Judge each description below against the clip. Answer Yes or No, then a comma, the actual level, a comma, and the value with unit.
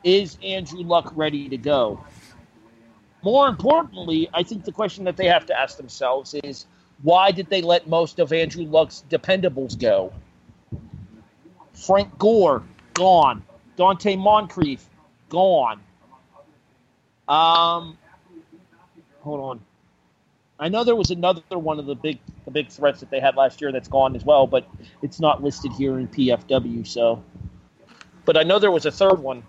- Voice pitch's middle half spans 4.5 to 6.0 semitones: Yes, wide, 5.4 semitones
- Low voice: No, medium, 155 Hz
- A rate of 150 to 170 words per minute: Yes, average, 155 wpm